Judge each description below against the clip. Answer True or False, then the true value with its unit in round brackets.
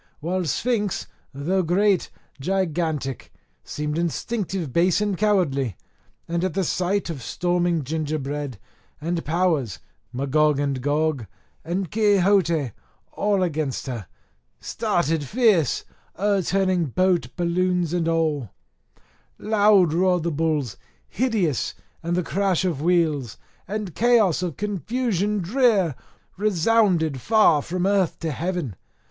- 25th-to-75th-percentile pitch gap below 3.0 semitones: False (4.3 semitones)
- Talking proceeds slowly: True (115 wpm)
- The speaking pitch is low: False (175 Hz)